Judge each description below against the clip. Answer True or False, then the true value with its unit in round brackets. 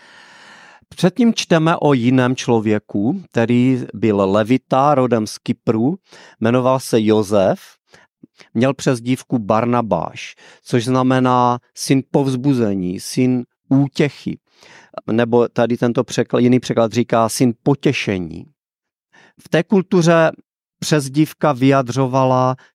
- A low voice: True (130 Hz)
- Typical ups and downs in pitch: True (3.6 semitones)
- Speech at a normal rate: False (100 wpm)